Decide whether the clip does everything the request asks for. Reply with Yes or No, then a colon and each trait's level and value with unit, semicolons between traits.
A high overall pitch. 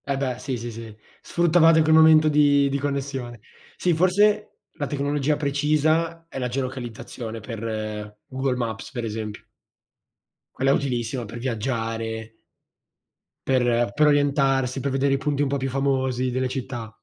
No: low, 135 Hz